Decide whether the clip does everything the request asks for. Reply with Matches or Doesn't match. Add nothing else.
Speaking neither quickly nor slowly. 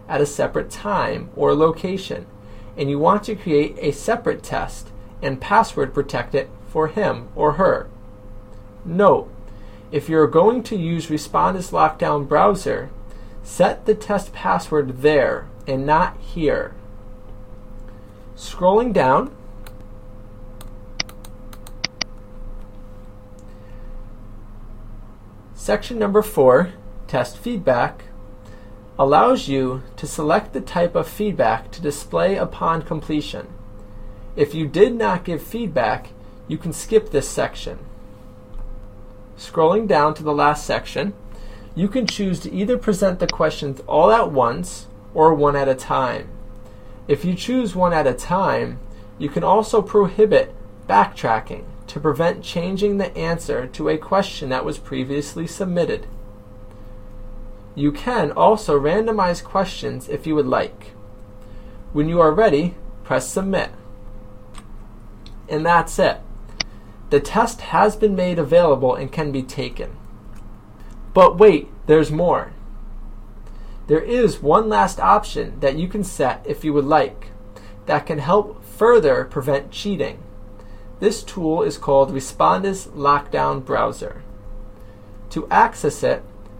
Doesn't match